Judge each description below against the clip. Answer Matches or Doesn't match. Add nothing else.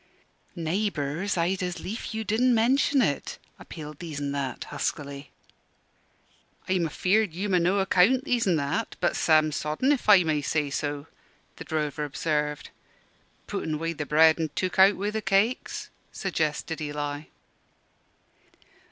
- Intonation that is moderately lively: Matches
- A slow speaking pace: Doesn't match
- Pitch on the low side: Doesn't match